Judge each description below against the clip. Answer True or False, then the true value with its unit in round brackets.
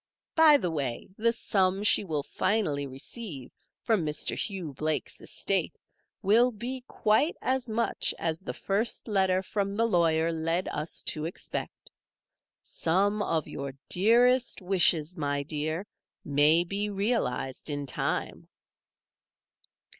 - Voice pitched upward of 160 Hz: True (185 Hz)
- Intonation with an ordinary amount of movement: False (5.7 semitones)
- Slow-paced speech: True (125 wpm)